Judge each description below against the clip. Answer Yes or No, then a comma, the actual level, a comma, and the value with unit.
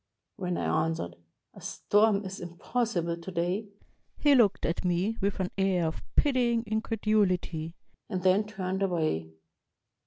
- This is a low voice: No, high, 190 Hz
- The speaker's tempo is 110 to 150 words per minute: Yes, slow, 135 wpm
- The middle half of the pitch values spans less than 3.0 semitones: No, average, 3.8 semitones